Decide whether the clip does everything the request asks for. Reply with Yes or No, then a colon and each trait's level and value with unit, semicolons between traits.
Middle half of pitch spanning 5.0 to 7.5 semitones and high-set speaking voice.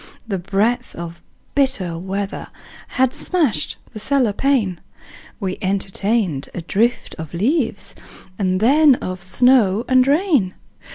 Yes: wide, 5.6 semitones; high, 210 Hz